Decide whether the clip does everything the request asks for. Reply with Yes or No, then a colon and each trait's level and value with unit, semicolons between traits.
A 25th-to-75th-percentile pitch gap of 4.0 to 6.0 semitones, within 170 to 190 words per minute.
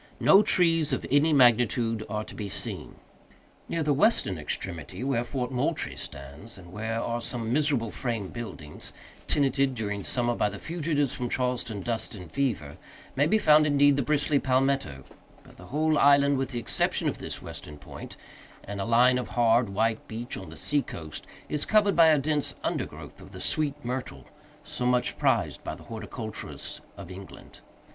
Yes: average, 4.9 semitones; average, 175 wpm